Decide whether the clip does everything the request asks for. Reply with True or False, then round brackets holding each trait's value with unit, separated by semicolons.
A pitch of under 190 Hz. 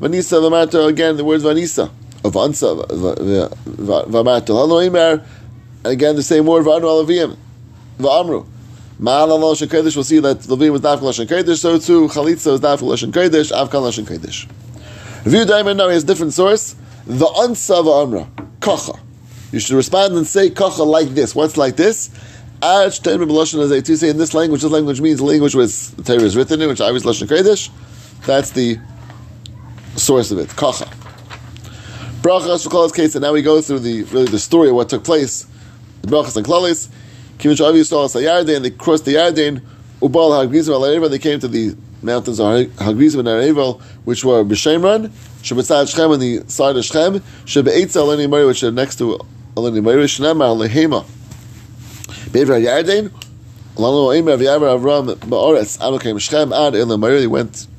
True (140 Hz)